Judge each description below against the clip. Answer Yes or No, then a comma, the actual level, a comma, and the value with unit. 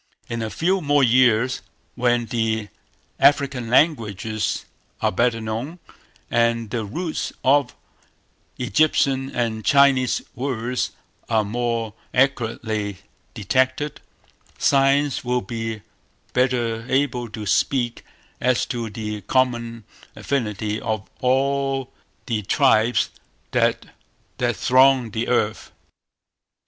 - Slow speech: Yes, slow, 100 wpm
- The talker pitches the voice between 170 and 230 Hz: No, low, 120 Hz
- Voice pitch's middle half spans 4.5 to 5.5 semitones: No, average, 3.2 semitones